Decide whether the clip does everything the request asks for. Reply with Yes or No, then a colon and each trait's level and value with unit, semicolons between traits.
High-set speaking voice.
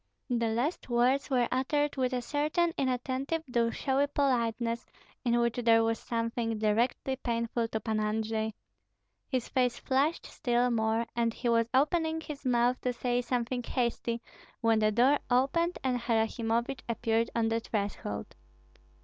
Yes: high, 240 Hz